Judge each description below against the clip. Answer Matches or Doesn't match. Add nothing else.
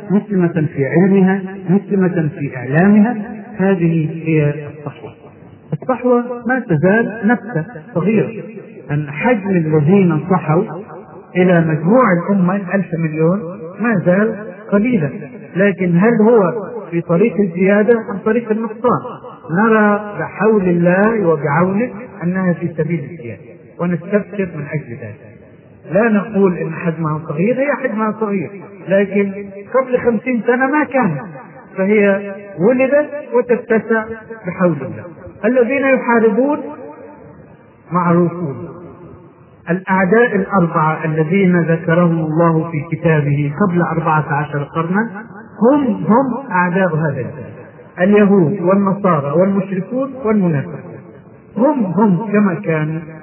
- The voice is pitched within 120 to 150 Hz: Doesn't match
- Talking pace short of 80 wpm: Doesn't match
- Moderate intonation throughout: Matches